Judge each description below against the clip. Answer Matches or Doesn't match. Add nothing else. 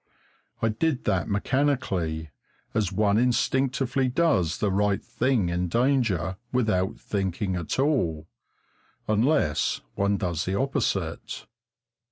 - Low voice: Matches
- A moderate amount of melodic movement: Doesn't match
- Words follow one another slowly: Matches